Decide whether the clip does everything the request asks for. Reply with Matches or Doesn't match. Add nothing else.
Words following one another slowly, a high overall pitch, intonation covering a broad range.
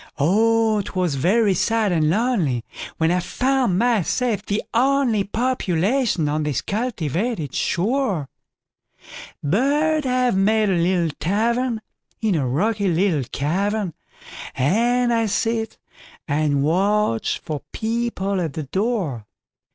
Matches